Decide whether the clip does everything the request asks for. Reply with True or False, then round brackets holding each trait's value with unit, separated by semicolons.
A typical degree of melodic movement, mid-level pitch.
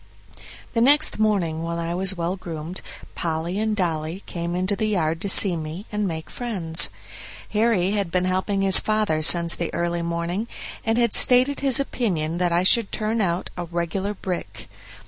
True (3.9 semitones; 180 Hz)